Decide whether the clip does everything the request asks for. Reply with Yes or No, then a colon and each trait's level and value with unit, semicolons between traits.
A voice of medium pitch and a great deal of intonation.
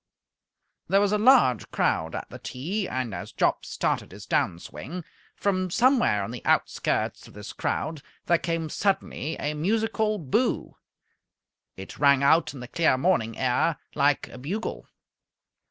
Yes: medium, 160 Hz; wide, 7.6 semitones